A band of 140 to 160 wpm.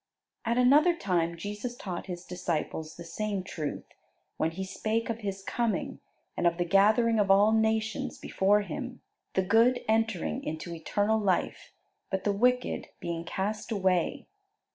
Yes: average, 150 wpm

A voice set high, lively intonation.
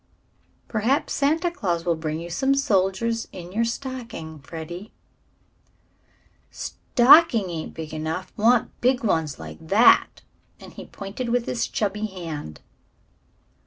Yes: high, 200 Hz; wide, 6.6 semitones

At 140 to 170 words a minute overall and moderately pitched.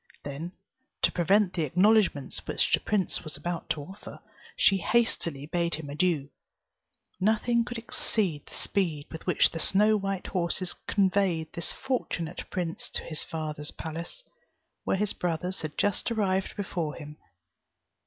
Yes: average, 145 wpm; medium, 175 Hz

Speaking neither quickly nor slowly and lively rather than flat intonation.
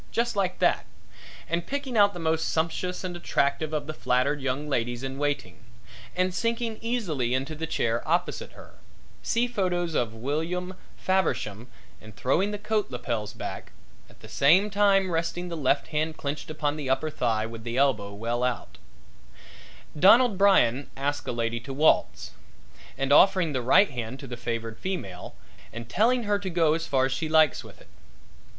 Yes: average, 175 wpm; wide, 6.5 semitones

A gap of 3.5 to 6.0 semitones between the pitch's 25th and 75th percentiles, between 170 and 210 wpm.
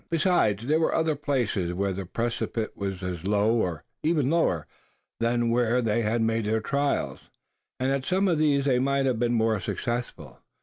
Yes: average, 4.9 semitones; average, 180 wpm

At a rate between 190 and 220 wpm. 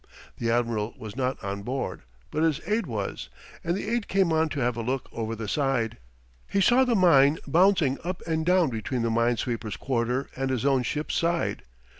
Yes: average, 200 wpm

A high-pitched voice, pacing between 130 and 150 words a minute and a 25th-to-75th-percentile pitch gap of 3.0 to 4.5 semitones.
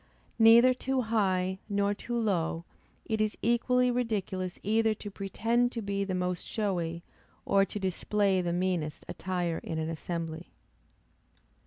Yes: high, 200 Hz; average, 140 wpm; average, 3.8 semitones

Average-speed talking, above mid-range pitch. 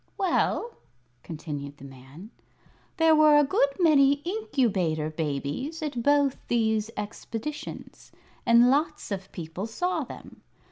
No: slow, 120 wpm; high, 235 Hz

